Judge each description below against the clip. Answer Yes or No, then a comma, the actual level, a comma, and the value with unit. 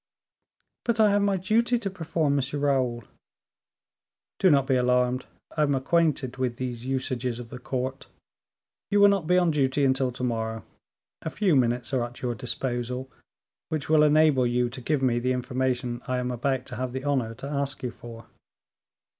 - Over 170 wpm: Yes, average, 180 wpm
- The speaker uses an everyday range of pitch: Yes, average, 3.3 semitones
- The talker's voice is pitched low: Yes, low, 130 Hz